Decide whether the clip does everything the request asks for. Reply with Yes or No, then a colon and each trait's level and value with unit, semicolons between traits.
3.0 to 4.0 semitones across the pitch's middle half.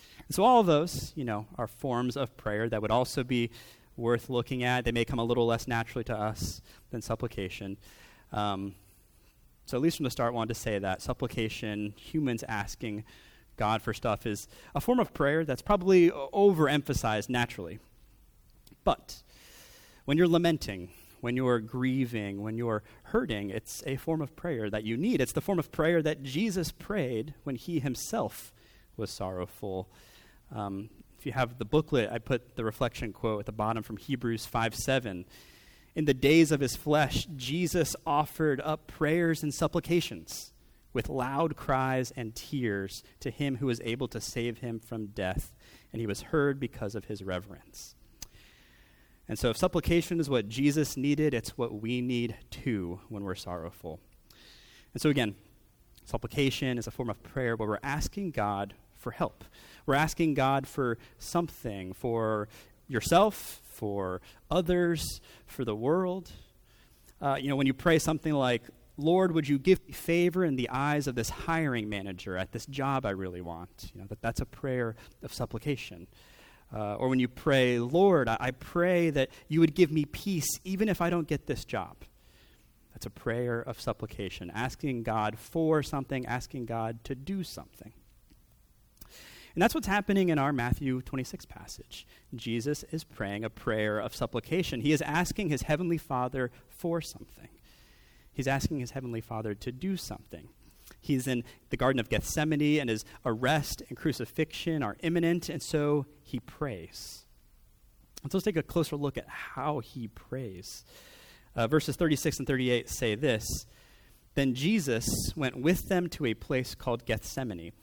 No: wide, 5.5 semitones